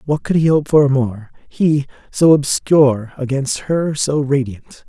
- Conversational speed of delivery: Yes, average, 150 wpm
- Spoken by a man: Yes, male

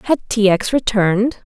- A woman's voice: Yes, female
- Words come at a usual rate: Yes, average, 160 wpm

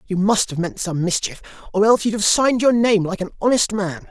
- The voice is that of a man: Yes, male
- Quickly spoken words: Yes, fast, 250 wpm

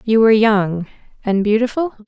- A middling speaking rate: Yes, average, 145 wpm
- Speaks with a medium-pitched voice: No, high, 220 Hz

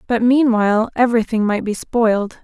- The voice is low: No, high, 225 Hz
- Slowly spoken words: No, average, 150 wpm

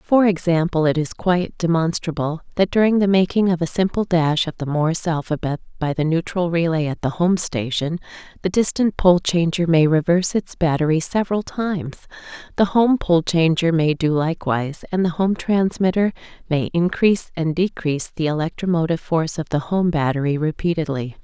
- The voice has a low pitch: No, medium, 170 Hz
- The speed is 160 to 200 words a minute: Yes, average, 165 wpm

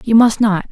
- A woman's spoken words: Yes, female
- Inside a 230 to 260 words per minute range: Yes, fast, 250 wpm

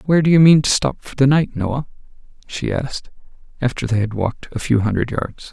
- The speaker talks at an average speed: No, fast, 215 wpm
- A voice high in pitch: No, low, 130 Hz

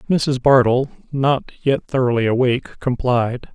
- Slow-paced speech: Yes, slow, 120 wpm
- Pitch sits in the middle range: No, low, 130 Hz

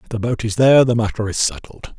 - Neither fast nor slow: No, fast, 270 wpm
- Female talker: No, male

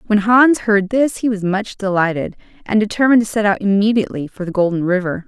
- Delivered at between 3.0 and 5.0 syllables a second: No, 6.0 syllables/s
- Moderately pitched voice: No, high, 205 Hz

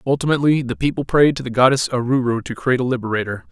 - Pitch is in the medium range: No, low, 130 Hz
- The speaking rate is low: No, fast, 205 wpm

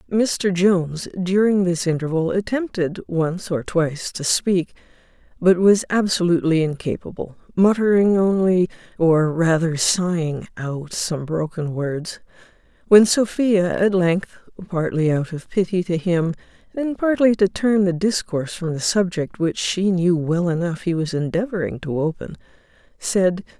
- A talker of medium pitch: Yes, medium, 180 Hz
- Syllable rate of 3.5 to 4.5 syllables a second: Yes, 4.4 syllables/s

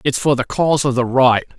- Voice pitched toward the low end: Yes, low, 130 Hz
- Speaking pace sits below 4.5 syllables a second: No, 5.9 syllables/s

